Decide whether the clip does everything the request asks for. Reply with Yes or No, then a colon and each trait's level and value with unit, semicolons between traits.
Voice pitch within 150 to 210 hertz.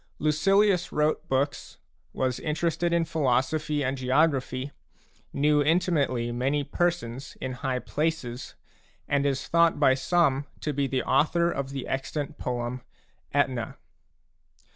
No: medium, 140 Hz